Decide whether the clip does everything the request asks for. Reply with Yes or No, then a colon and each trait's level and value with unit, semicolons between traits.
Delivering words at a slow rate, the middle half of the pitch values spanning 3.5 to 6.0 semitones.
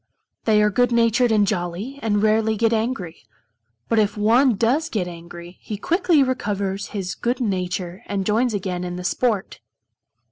No: average, 165 wpm; average, 4.0 semitones